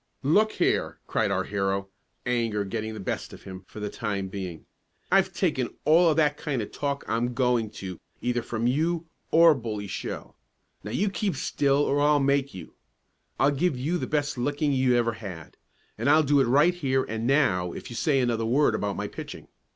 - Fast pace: No, average, 195 wpm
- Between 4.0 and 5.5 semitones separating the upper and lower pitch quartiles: Yes, average, 5.2 semitones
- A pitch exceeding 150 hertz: No, low, 125 Hz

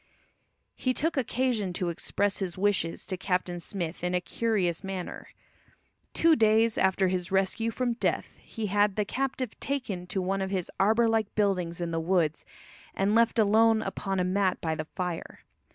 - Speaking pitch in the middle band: No, high, 195 Hz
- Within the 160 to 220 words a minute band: Yes, average, 170 wpm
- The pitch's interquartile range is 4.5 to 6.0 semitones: No, average, 3.6 semitones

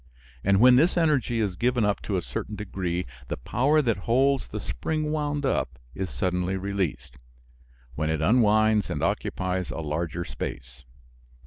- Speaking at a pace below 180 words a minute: Yes, average, 155 wpm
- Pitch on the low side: Yes, low, 100 Hz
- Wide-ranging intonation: Yes, wide, 6.1 semitones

